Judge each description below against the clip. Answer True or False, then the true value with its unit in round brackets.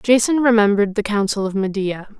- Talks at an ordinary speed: True (165 wpm)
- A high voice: True (210 Hz)